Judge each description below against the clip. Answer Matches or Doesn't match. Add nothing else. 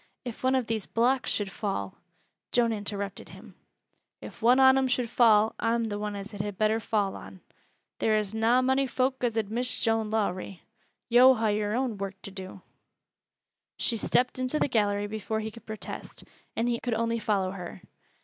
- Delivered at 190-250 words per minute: Matches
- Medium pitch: Doesn't match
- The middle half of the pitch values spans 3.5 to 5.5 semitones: Doesn't match